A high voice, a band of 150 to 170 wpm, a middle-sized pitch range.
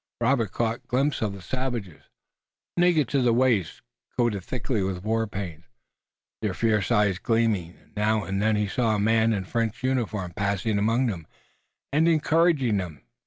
No: low, 110 Hz; average, 165 wpm; average, 3.8 semitones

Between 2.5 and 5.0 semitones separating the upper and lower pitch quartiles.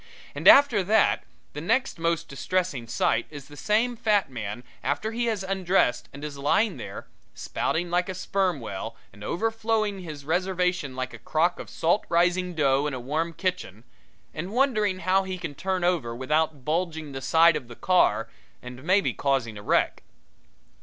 No: wide, 5.5 semitones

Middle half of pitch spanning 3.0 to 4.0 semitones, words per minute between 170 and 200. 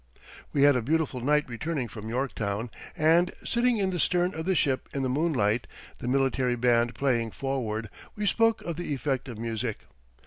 No: wide, 5.5 semitones; average, 180 wpm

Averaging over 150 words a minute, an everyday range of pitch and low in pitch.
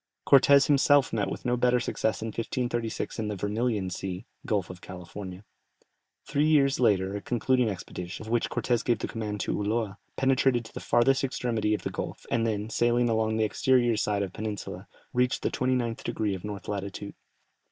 Yes: average, 185 wpm; average, 3.3 semitones; low, 110 Hz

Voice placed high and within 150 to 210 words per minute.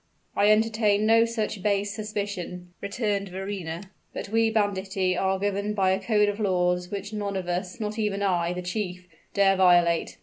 Yes: high, 200 Hz; average, 170 wpm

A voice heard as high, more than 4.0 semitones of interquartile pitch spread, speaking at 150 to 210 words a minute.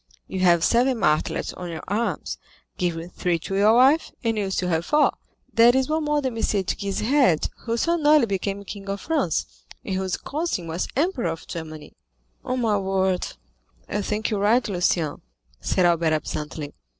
Yes: high, 200 Hz; wide, 5.6 semitones; average, 185 wpm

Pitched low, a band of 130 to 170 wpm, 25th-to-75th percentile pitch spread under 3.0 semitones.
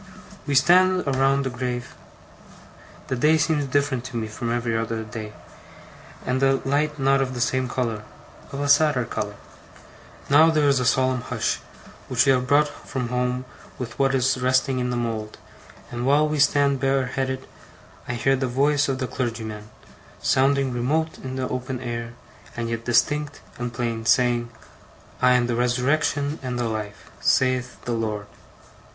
Yes: low, 130 Hz; average, 165 wpm; narrow, 2.4 semitones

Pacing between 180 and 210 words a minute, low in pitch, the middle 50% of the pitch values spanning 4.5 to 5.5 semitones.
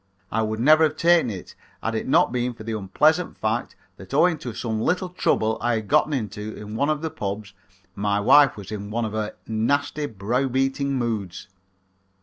Yes: average, 195 wpm; low, 115 Hz; average, 5.0 semitones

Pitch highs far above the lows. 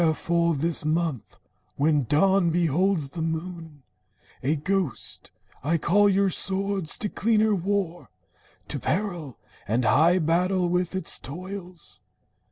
No: average, 3.4 semitones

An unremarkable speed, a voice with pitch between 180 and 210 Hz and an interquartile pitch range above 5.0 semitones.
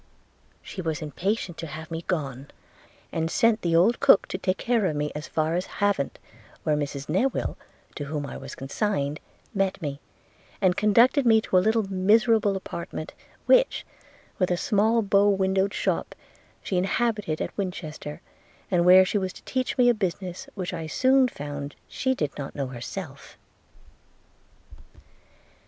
Yes: average, 160 wpm; medium, 185 Hz; wide, 5.4 semitones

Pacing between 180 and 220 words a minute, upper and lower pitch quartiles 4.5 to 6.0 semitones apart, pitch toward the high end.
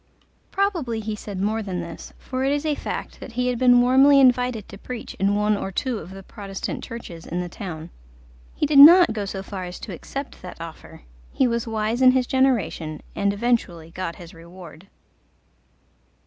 Yes: average, 190 wpm; wide, 5.5 semitones; high, 215 Hz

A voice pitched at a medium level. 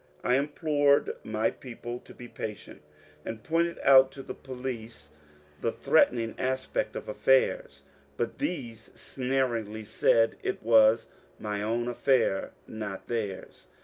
No: low, 120 Hz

